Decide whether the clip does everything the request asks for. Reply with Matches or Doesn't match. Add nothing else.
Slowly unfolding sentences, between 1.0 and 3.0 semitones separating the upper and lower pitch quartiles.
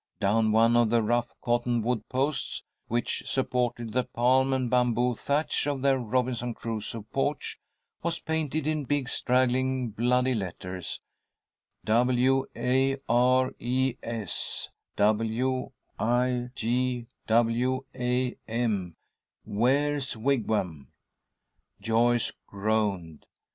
Matches